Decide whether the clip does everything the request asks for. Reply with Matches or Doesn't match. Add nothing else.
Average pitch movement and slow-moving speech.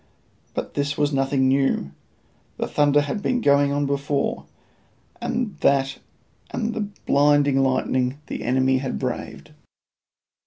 Doesn't match